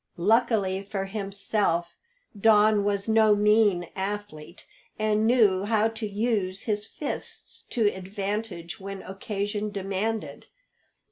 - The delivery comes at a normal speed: No, slow, 110 wpm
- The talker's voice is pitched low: No, high, 205 Hz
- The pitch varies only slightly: Yes, narrow, 2.0 semitones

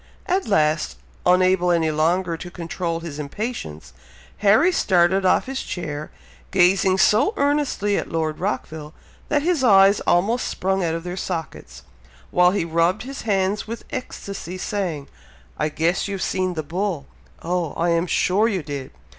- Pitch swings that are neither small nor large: Yes, average, 3.5 semitones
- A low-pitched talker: No, medium, 180 Hz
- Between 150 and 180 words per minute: Yes, average, 155 wpm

